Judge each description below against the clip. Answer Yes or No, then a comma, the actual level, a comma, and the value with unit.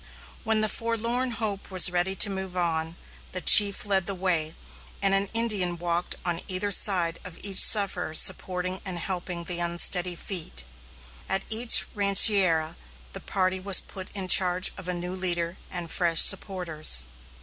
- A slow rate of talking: No, average, 160 wpm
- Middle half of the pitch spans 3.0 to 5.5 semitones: No, narrow, 2.4 semitones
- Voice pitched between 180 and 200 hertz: Yes, medium, 185 Hz